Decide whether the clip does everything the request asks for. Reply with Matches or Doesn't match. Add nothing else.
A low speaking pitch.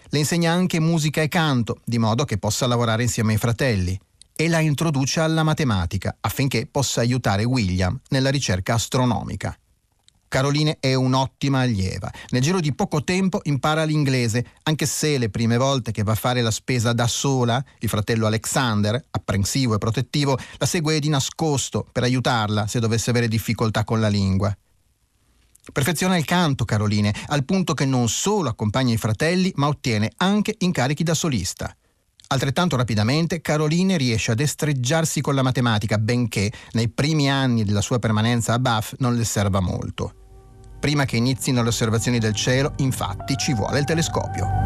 Matches